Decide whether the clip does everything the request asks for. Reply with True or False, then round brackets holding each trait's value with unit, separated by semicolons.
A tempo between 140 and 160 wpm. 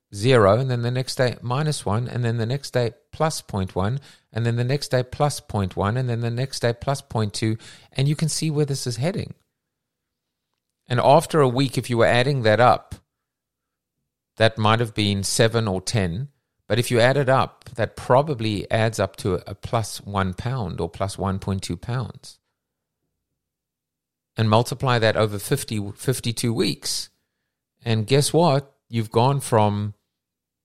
False (175 wpm)